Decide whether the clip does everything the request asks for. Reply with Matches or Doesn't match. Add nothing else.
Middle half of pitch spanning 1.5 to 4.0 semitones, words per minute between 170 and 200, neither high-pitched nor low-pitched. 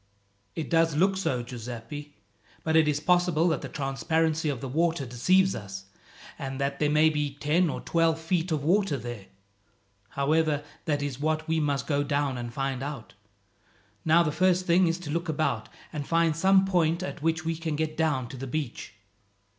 Matches